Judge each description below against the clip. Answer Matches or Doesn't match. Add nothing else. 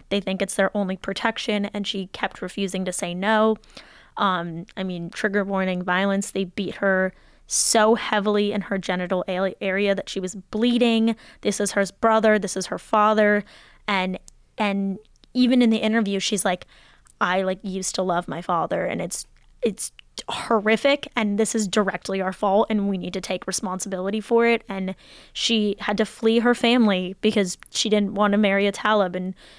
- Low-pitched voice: Doesn't match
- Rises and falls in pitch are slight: Matches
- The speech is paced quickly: Doesn't match